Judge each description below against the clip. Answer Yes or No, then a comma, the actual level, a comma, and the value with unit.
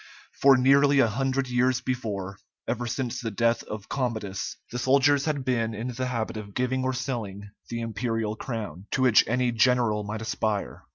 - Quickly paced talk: No, average, 175 wpm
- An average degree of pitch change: Yes, average, 3.0 semitones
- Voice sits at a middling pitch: No, low, 120 Hz